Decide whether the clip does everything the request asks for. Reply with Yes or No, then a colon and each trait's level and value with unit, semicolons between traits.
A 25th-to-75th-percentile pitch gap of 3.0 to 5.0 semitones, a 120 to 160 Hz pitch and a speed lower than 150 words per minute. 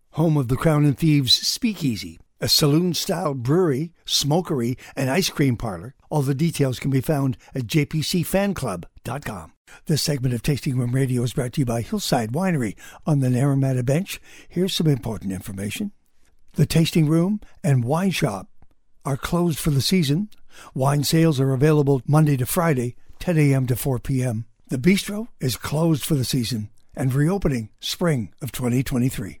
No: average, 4.3 semitones; medium, 140 Hz; average, 160 wpm